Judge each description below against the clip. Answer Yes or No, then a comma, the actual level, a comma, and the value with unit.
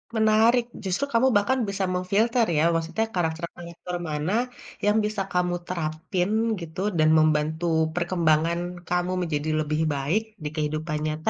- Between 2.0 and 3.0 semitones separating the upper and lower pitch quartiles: No, average, 3.9 semitones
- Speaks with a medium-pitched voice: Yes, medium, 170 Hz